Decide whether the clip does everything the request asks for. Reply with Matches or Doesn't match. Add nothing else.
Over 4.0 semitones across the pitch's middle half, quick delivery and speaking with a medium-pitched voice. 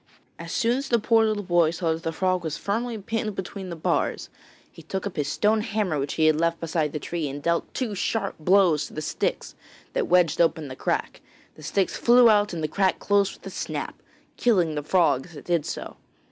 Matches